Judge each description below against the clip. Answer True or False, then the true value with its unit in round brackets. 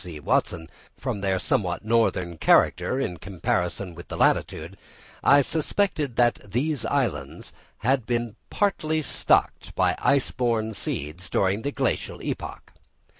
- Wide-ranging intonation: True (7.1 semitones)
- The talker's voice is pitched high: False (110 Hz)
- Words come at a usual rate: False (130 wpm)